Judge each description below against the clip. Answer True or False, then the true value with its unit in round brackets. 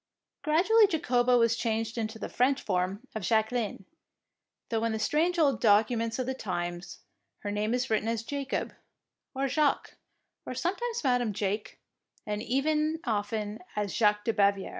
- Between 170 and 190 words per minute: False (155 wpm)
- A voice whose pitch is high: True (225 Hz)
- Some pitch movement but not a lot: True (4.0 semitones)